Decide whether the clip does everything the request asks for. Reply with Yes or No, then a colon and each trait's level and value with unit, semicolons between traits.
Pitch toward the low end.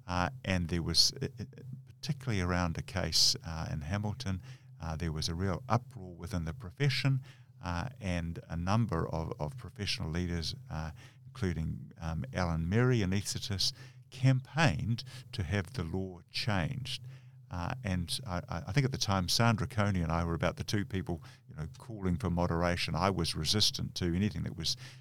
Yes: low, 100 Hz